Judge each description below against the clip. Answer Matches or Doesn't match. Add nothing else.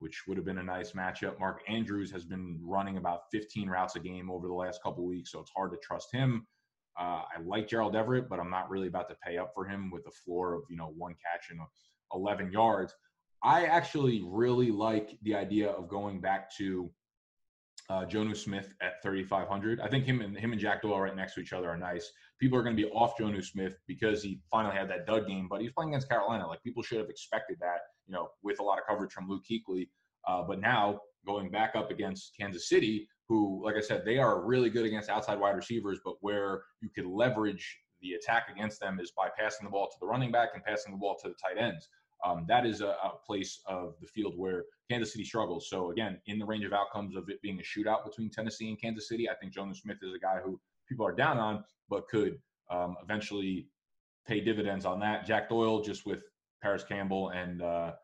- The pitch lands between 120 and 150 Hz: Doesn't match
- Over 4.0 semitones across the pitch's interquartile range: Doesn't match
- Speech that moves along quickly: Matches